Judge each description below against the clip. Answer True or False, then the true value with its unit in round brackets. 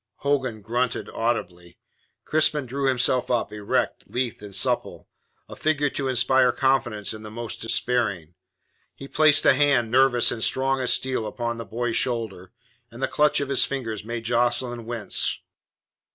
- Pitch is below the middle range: True (120 Hz)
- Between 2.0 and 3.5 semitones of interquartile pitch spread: True (2.9 semitones)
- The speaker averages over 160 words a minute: False (155 wpm)